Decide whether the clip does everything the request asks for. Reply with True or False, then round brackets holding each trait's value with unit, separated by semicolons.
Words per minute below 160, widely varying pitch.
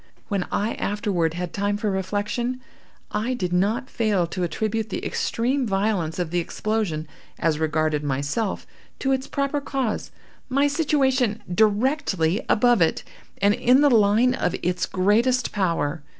True (140 wpm; 5.7 semitones)